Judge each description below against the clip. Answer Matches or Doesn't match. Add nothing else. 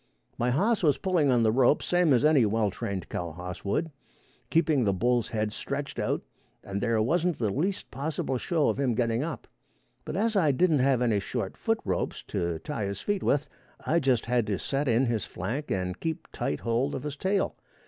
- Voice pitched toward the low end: Matches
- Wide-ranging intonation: Matches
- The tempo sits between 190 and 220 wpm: Matches